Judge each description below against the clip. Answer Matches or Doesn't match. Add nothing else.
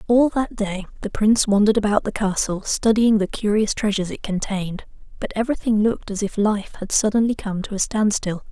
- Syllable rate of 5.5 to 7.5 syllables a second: Matches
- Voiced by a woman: Matches